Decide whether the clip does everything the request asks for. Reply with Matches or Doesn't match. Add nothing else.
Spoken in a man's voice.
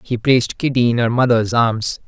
Matches